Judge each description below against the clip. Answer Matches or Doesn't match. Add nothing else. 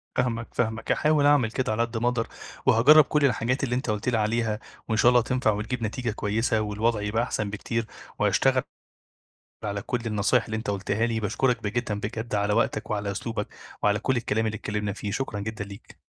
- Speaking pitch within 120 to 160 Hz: Doesn't match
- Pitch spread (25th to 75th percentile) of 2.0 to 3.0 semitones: Matches